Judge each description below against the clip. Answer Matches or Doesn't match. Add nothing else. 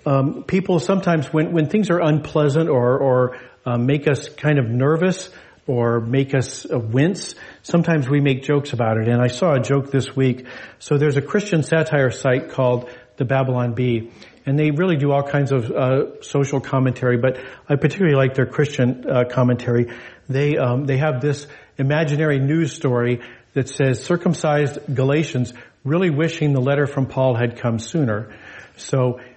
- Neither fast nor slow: Matches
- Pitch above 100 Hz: Matches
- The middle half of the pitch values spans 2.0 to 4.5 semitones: Matches